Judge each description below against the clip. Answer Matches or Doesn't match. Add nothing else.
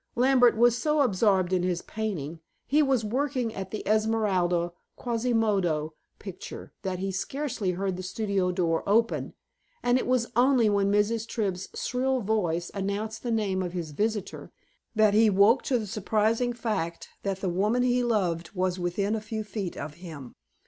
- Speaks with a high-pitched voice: Matches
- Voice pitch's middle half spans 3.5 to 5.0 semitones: Matches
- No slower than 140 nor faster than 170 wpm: Matches